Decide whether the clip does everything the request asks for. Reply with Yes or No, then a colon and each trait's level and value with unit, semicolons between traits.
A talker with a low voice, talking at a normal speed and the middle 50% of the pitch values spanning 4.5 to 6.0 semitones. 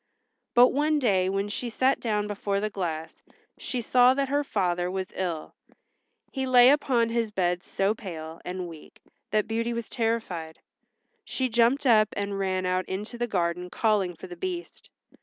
No: high, 210 Hz; average, 170 wpm; average, 4.8 semitones